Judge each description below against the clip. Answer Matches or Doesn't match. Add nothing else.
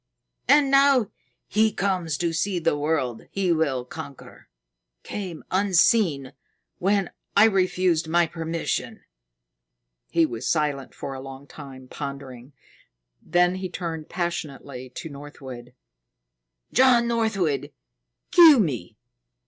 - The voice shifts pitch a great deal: Matches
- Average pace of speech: Doesn't match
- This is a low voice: Doesn't match